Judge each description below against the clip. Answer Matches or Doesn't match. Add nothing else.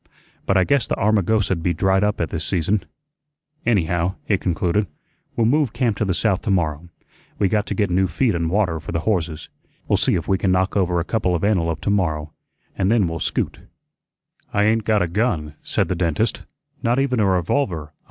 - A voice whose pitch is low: Matches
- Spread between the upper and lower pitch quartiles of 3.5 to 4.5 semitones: Matches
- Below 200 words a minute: Doesn't match